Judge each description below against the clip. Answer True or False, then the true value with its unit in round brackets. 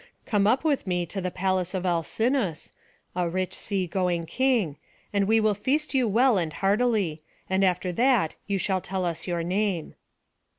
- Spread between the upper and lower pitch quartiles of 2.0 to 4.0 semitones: True (3.7 semitones)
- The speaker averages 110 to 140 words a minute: False (175 wpm)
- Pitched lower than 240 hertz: True (190 Hz)